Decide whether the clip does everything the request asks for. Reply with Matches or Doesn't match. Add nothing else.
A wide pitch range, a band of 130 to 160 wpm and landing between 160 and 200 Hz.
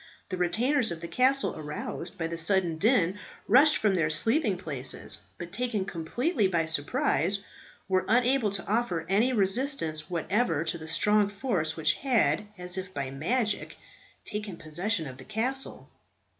Matches